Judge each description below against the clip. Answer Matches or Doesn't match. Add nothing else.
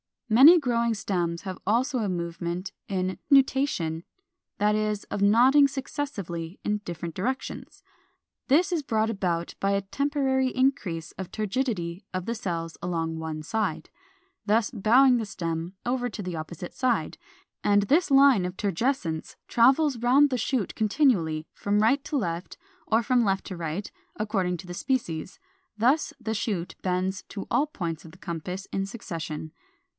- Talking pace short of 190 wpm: Matches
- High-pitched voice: Matches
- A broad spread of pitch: Matches